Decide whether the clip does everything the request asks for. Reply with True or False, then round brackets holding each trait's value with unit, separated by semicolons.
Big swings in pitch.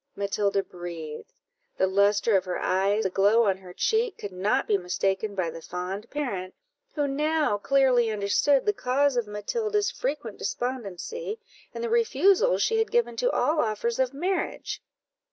True (7.6 semitones)